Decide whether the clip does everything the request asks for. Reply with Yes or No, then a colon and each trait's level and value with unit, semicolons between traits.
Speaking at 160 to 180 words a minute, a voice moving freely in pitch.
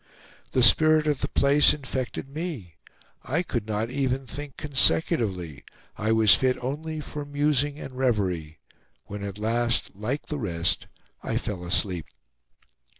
No: average, 140 wpm; wide, 5.8 semitones